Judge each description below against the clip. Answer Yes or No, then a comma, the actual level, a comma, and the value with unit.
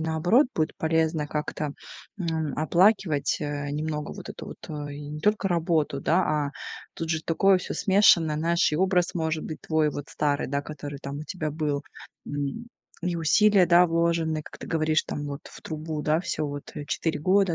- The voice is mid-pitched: Yes, medium, 160 Hz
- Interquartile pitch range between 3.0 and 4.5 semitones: No, narrow, 2.4 semitones